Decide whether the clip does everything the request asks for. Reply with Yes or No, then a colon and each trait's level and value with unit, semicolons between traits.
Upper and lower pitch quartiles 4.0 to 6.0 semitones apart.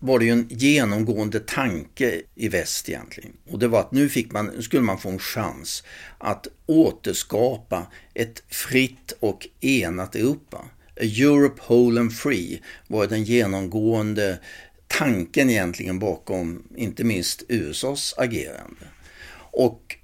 Yes: average, 4.3 semitones